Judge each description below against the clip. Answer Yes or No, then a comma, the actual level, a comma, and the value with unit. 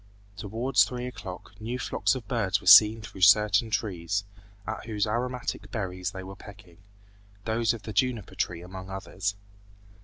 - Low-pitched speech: Yes, low, 105 Hz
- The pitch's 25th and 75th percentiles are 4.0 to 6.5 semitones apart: No, average, 3.1 semitones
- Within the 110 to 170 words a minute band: Yes, average, 155 wpm